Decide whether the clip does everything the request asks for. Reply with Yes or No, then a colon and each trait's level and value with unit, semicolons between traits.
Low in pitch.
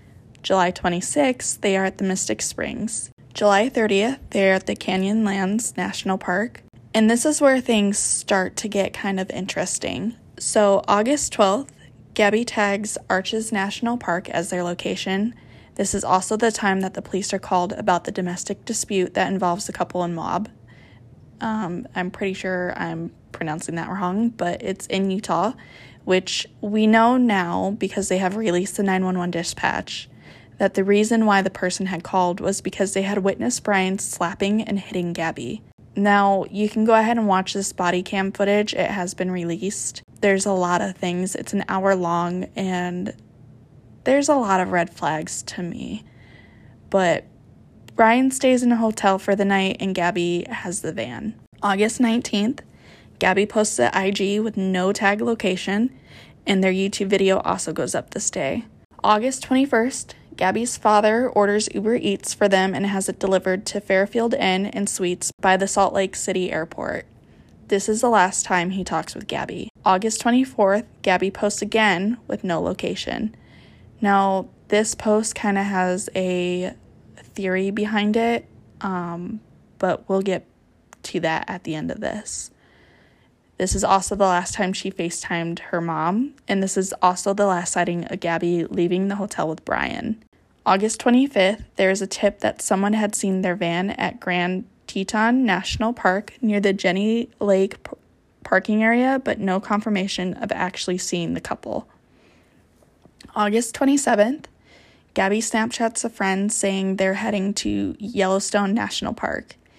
No: high, 195 Hz